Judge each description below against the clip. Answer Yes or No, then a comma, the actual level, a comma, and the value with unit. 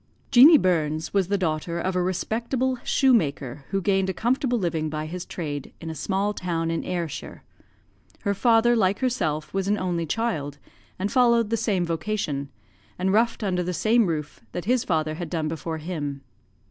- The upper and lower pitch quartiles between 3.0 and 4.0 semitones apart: No, wide, 5.4 semitones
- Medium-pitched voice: Yes, medium, 180 Hz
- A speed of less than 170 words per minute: No, average, 175 wpm